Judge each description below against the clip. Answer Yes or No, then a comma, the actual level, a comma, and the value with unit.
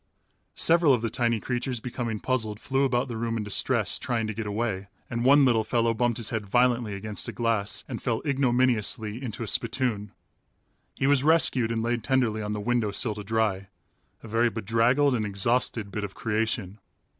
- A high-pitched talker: No, low, 115 Hz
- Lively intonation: No, average, 2.7 semitones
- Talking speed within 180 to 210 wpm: Yes, average, 190 wpm